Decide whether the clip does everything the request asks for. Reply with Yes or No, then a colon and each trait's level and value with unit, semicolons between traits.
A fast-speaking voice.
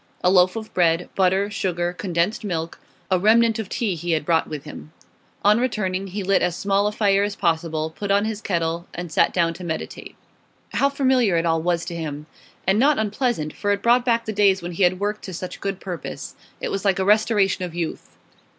Yes: fast, 215 wpm